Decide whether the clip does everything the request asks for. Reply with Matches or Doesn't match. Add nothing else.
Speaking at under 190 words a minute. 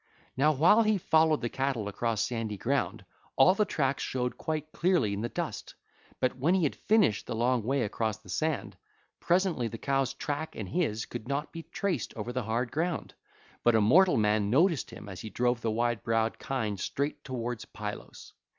Doesn't match